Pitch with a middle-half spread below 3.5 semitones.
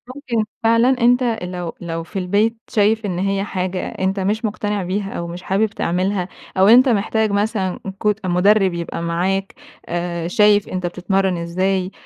Yes: average, 2.9 semitones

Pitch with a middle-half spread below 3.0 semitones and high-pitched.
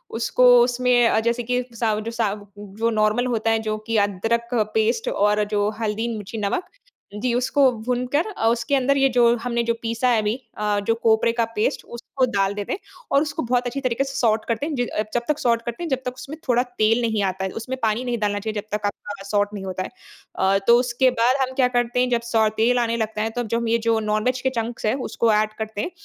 Yes: narrow, 2.6 semitones; high, 230 Hz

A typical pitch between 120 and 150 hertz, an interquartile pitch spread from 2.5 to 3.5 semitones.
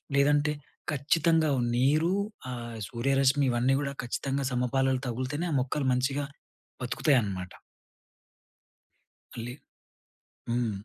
Yes: low, 135 Hz; average, 2.9 semitones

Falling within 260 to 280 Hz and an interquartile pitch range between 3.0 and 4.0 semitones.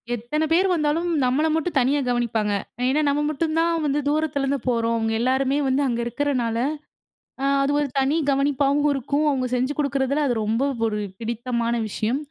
Yes: very high, 275 Hz; average, 3.5 semitones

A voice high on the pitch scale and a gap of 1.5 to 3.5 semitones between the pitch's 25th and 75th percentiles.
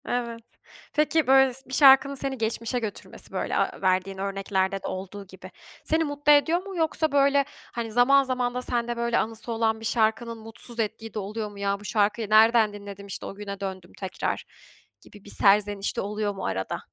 No: high, 225 Hz; average, 4.0 semitones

